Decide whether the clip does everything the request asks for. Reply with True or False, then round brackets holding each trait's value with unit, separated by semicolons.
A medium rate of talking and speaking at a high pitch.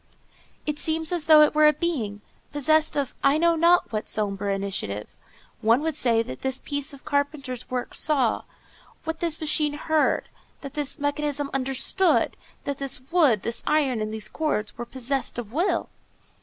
True (170 wpm; 280 Hz)